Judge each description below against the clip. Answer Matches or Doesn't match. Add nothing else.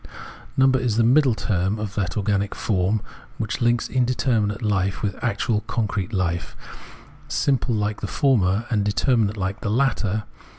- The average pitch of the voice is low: Matches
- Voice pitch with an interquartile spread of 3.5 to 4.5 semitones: Doesn't match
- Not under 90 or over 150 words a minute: Matches